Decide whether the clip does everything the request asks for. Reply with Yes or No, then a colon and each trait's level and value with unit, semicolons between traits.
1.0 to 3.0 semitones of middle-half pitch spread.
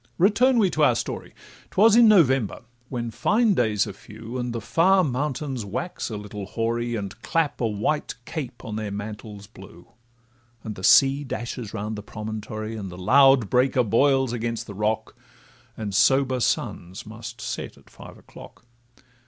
No: average, 4.3 semitones